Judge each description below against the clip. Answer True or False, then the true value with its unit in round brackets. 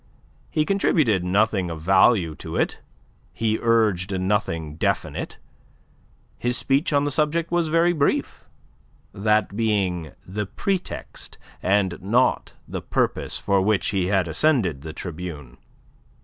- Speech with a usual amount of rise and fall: False (6.3 semitones)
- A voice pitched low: True (105 Hz)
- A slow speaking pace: True (125 wpm)